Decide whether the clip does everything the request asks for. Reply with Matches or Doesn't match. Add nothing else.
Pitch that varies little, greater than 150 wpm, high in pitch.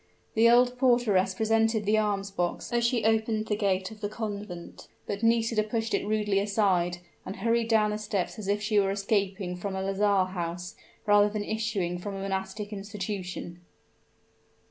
Matches